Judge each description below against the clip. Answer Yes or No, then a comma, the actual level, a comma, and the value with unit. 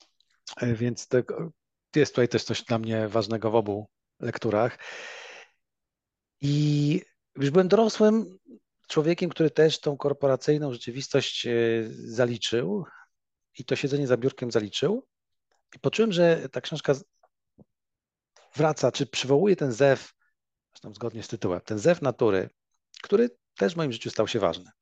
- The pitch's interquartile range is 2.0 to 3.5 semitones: No, average, 5.2 semitones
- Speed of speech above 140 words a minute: No, average, 130 wpm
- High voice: No, low, 135 Hz